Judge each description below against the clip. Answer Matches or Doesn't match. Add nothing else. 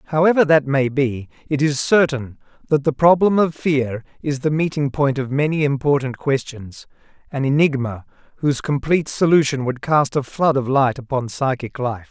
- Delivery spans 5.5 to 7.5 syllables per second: Doesn't match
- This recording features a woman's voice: Doesn't match